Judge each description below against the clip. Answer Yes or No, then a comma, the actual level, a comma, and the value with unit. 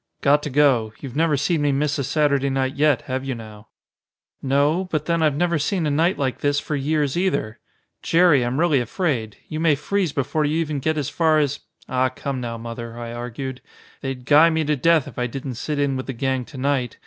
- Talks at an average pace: No, fast, 225 wpm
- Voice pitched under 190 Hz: Yes, medium, 140 Hz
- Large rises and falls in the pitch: No, average, 3.1 semitones